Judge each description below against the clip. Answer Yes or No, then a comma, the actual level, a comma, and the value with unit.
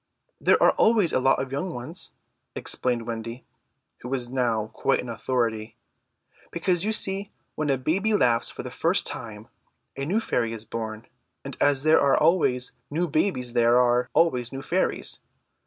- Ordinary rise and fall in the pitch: No, wide, 5.7 semitones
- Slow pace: No, average, 170 wpm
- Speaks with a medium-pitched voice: No, low, 130 Hz